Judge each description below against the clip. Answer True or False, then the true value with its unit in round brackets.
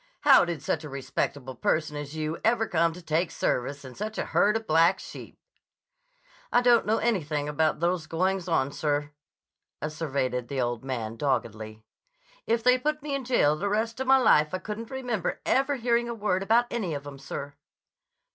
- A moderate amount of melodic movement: False (7.8 semitones)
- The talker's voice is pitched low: False (165 Hz)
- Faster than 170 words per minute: True (185 wpm)